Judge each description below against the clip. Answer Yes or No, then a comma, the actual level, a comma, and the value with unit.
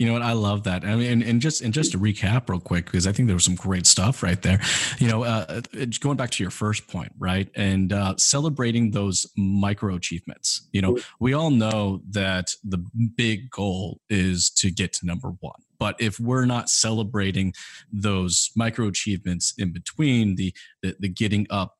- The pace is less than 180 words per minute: No, average, 200 wpm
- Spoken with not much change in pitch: No, average, 3.7 semitones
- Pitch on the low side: Yes, low, 100 Hz